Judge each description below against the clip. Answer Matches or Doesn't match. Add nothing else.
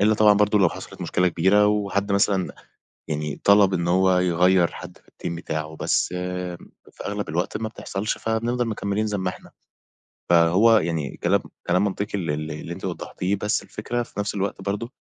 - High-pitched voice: Doesn't match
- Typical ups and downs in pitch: Matches